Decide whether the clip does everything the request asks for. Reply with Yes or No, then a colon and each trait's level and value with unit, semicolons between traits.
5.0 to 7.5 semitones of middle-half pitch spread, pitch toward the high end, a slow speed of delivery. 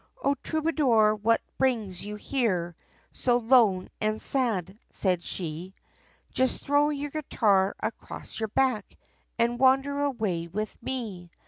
Yes: wide, 5.4 semitones; high, 225 Hz; slow, 125 wpm